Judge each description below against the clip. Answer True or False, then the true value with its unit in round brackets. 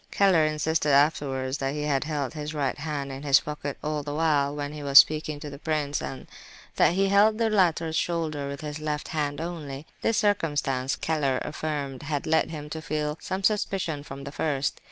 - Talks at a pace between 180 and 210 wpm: True (200 wpm)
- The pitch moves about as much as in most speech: False (2.2 semitones)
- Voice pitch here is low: False (150 Hz)